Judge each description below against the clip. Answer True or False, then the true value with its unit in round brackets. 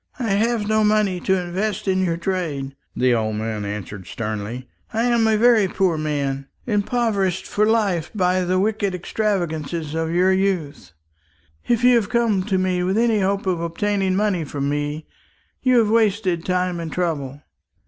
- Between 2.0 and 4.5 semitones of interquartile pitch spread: False (5.1 semitones)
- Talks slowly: False (170 wpm)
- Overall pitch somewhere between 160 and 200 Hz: True (185 Hz)